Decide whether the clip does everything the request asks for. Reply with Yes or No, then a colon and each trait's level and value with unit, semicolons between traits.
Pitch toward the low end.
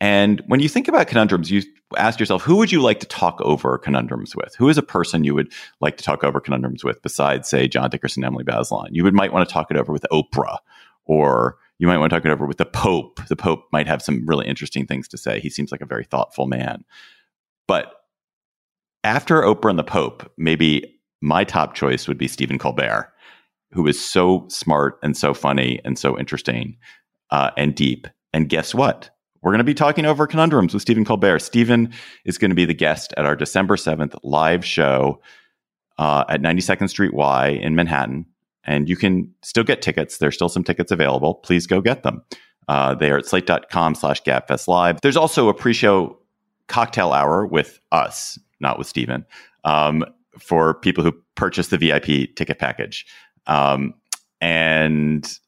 Yes: very low, 80 Hz